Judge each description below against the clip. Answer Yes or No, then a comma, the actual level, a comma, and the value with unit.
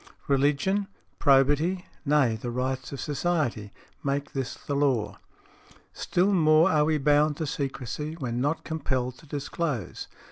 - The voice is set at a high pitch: No, medium, 145 Hz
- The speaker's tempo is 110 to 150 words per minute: Yes, average, 140 wpm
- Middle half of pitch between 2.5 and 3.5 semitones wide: Yes, average, 2.9 semitones